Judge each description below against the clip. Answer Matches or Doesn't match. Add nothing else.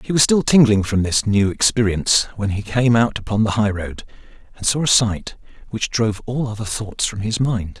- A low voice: Matches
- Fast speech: Matches